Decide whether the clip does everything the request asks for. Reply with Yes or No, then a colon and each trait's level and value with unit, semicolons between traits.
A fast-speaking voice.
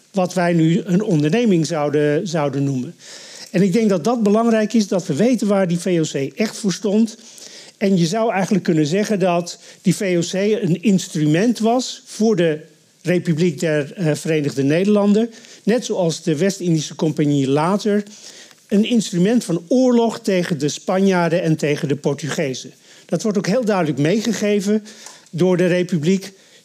No: average, 155 wpm